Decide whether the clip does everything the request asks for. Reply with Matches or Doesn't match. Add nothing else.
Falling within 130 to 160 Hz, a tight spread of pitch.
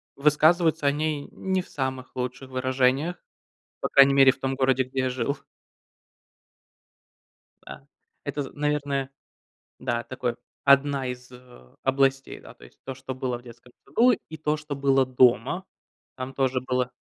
Matches